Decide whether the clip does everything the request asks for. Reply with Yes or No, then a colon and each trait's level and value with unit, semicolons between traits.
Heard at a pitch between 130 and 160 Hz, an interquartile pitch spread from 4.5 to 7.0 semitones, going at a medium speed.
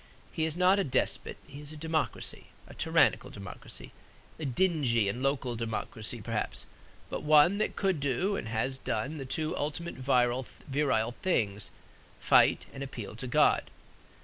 Yes: low, 135 Hz; average, 5.0 semitones; average, 150 wpm